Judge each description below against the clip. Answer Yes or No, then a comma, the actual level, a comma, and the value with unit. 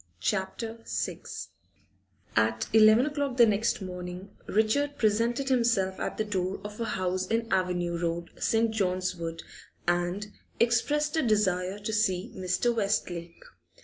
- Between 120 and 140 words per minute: Yes, slow, 135 wpm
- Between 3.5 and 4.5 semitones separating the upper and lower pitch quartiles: Yes, average, 4.0 semitones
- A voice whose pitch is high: Yes, high, 205 Hz